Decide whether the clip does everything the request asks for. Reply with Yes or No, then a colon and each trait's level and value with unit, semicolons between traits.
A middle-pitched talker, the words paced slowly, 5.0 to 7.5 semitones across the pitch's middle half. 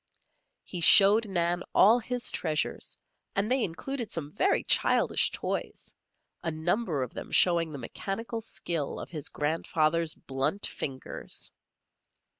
Yes: medium, 170 Hz; slow, 125 wpm; wide, 5.4 semitones